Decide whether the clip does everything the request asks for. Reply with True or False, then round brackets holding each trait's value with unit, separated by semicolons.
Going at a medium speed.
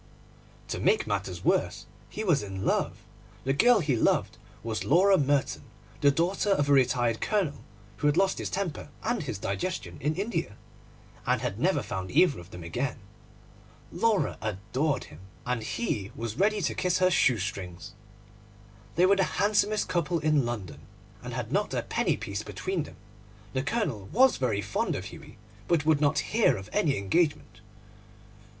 True (170 wpm)